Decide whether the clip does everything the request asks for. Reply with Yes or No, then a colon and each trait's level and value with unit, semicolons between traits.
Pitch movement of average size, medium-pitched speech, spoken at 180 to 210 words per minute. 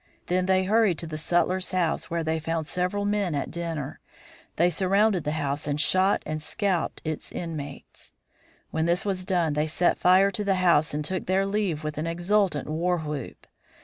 Yes: average, 3.3 semitones; medium, 175 Hz; average, 185 wpm